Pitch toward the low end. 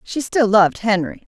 No: high, 215 Hz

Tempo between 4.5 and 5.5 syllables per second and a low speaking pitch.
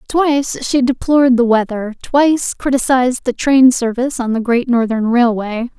No: 5.0 syllables/s; very high, 250 Hz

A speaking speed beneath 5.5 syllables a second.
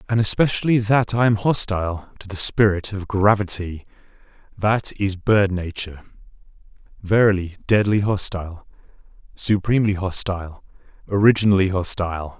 Yes: 5.2 syllables/s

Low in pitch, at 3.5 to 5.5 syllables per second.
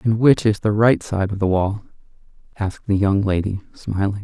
Yes: low, 105 Hz; 5.2 syllables/s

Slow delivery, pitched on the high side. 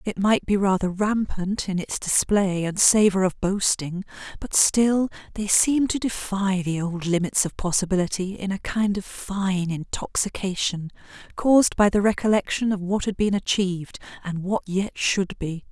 No: average, 165 wpm; high, 195 Hz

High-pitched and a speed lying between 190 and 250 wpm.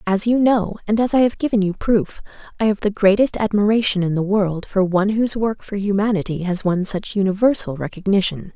Yes: high, 200 Hz; fast, 205 wpm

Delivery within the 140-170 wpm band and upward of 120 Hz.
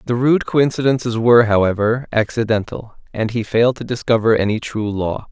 No: average, 160 wpm; low, 115 Hz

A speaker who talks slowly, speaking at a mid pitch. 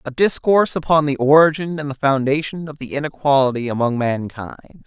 No: average, 160 wpm; medium, 145 Hz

